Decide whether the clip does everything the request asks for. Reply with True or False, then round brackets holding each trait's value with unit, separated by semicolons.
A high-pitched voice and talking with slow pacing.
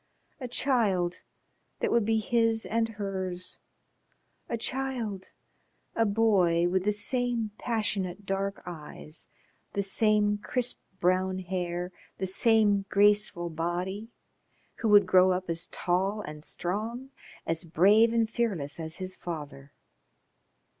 True (195 Hz; 120 wpm)